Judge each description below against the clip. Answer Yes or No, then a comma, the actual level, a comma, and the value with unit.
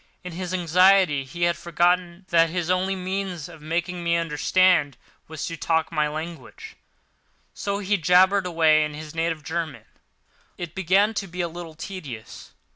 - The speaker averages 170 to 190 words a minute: No, average, 160 wpm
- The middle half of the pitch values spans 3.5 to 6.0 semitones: No, narrow, 2.4 semitones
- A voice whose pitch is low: No, medium, 170 Hz